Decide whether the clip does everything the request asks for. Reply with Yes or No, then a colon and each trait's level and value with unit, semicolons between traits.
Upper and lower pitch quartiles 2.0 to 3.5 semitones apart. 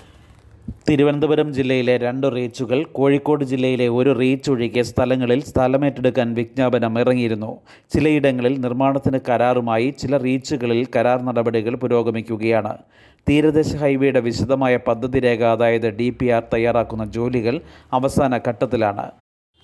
Yes: narrow, 2.5 semitones